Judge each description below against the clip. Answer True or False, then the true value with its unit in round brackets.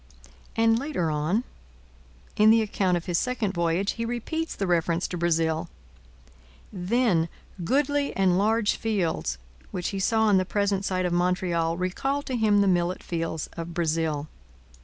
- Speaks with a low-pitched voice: False (185 Hz)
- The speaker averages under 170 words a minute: True (155 wpm)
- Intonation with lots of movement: False (4.6 semitones)